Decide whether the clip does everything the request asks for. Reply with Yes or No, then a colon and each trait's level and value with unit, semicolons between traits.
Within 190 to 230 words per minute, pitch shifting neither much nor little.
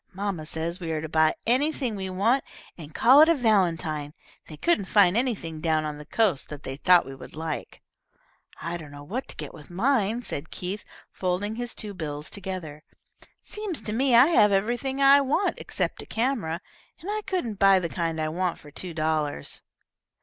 No: average, 195 wpm; wide, 7.0 semitones